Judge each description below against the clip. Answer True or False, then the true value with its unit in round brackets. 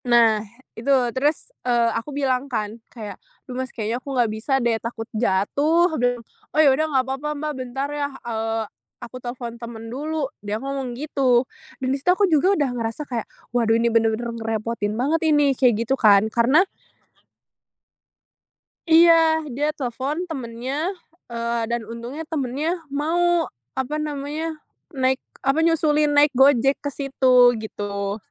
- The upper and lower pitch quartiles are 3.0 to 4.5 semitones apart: True (4.2 semitones)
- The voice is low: False (260 Hz)